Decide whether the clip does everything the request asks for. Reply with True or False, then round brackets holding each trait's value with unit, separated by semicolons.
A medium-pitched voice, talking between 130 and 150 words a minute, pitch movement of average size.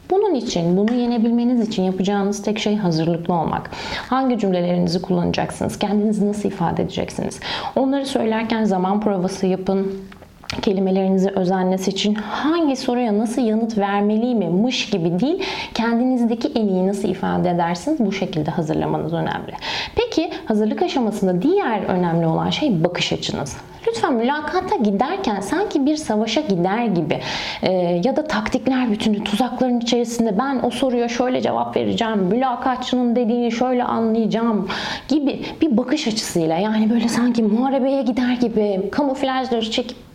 False (225 Hz; 135 wpm; 4.7 semitones)